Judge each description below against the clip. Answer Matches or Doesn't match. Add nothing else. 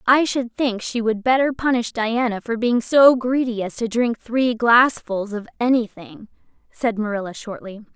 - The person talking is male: Doesn't match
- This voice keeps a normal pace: Matches